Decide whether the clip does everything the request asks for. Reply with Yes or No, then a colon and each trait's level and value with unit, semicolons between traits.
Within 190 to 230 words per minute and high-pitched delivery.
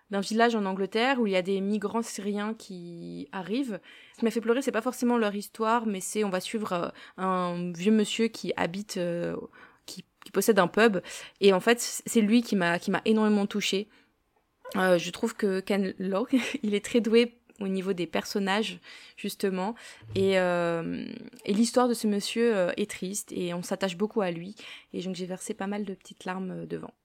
Yes: average, 200 wpm; high, 205 Hz